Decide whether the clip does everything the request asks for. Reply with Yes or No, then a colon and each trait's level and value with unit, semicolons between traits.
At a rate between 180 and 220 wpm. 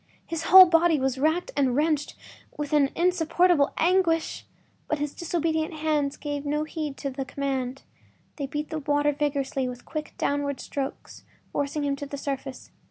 No: average, 165 wpm